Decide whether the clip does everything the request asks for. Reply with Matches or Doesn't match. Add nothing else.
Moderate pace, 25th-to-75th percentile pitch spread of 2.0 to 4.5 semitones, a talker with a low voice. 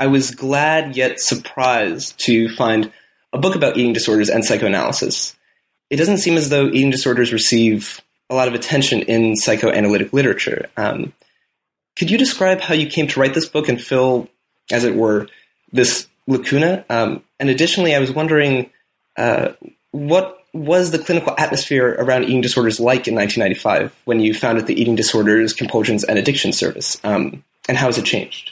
Doesn't match